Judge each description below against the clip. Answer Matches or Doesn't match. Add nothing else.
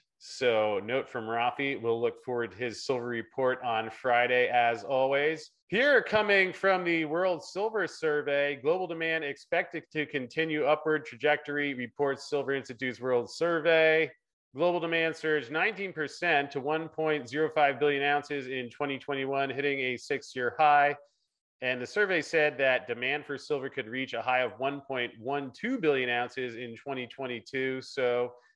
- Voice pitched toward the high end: Doesn't match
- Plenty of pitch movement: Doesn't match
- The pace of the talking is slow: Doesn't match